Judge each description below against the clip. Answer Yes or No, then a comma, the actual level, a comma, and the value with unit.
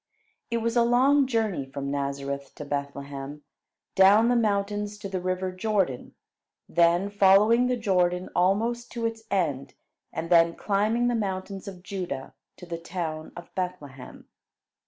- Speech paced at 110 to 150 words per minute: Yes, average, 145 wpm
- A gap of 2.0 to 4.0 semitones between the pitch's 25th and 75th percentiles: No, average, 5.2 semitones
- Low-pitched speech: No, high, 190 Hz